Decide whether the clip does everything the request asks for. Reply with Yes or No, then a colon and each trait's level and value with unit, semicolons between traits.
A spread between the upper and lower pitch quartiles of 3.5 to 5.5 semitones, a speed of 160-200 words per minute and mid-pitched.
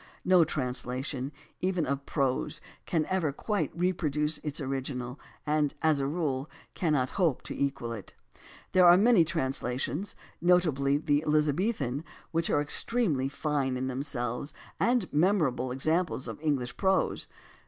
No: average, 4.5 semitones; slow, 135 wpm; medium, 150 Hz